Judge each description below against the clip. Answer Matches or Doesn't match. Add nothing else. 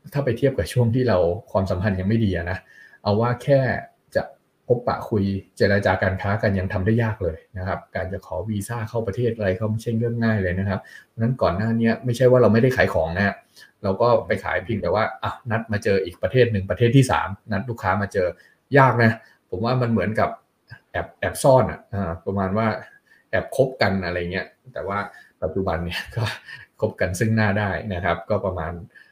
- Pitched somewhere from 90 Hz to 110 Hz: Matches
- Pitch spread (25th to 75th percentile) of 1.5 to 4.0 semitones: Matches